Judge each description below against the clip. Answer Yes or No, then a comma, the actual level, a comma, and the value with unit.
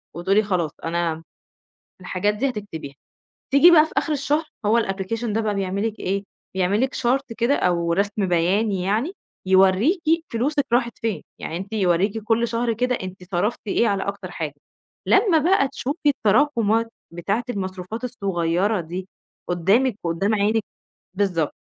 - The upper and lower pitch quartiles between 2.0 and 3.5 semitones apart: No, average, 4.3 semitones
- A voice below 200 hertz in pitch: No, high, 205 Hz